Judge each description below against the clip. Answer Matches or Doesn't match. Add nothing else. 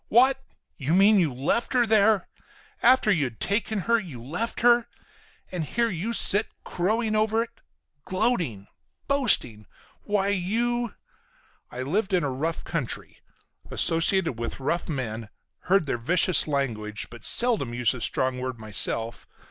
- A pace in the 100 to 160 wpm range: Matches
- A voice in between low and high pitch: Matches